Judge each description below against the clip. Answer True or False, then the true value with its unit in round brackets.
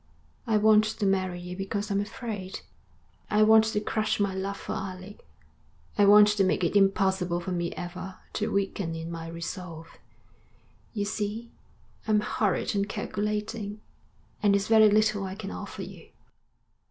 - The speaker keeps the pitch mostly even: True (2.2 semitones)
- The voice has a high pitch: True (200 Hz)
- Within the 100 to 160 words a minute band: True (155 wpm)